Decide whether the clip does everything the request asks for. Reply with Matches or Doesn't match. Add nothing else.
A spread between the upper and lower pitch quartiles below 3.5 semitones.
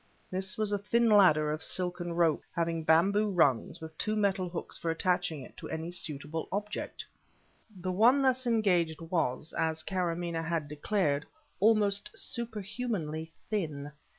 Doesn't match